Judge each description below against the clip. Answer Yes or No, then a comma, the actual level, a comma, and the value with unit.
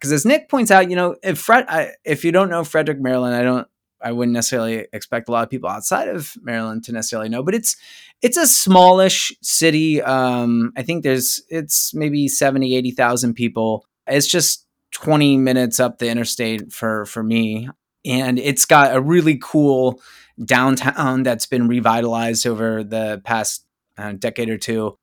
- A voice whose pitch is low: Yes, low, 130 Hz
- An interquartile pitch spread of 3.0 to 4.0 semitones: No, average, 5.2 semitones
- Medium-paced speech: Yes, average, 175 wpm